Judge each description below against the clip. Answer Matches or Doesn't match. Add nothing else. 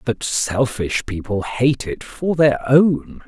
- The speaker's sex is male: Matches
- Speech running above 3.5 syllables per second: Doesn't match